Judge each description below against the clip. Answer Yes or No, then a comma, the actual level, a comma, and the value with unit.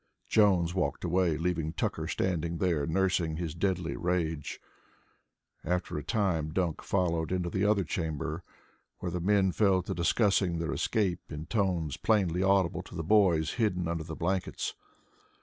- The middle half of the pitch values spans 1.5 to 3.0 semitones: Yes, average, 2.7 semitones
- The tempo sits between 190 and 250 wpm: No, average, 150 wpm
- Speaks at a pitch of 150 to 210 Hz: No, very low, 90 Hz